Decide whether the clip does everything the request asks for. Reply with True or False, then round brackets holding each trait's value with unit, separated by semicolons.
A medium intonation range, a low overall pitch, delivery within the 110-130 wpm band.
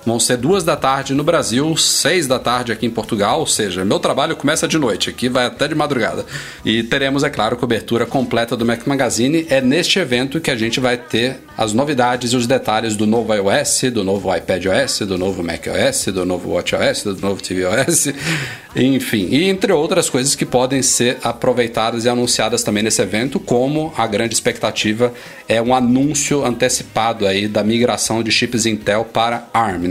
False (3.5 semitones; 120 Hz; 185 wpm)